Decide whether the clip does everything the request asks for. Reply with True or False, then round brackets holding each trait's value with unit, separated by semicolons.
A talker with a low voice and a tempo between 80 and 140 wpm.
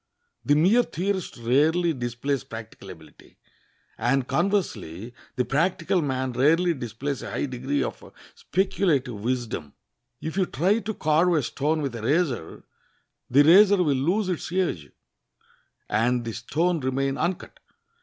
False (145 Hz; 135 wpm)